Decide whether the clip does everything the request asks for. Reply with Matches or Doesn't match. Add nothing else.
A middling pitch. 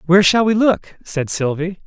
Matches